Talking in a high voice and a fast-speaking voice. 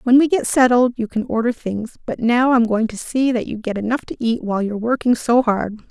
Yes: high, 235 Hz; fast, 255 wpm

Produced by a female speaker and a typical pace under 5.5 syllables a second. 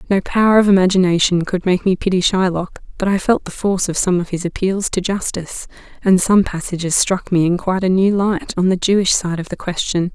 No: female; 5.8 syllables/s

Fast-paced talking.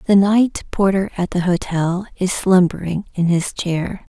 No: average, 160 wpm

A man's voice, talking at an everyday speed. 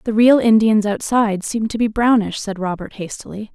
No: female; average, 185 wpm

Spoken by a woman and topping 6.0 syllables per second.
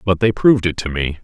No: male; 6.4 syllables/s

